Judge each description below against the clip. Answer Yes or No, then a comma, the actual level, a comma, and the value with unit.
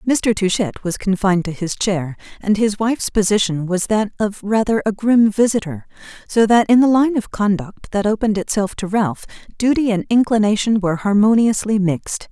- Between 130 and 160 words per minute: No, average, 175 wpm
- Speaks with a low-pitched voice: No, high, 210 Hz